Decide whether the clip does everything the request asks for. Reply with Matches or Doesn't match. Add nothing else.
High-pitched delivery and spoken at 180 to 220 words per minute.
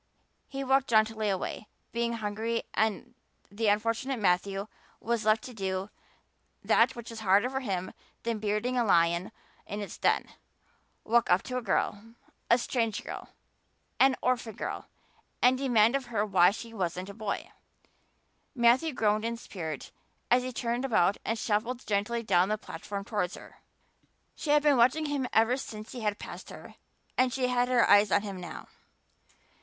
Doesn't match